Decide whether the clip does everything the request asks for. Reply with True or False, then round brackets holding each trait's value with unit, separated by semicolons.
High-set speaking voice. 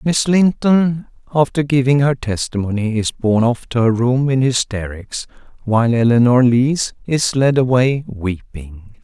False (125 Hz)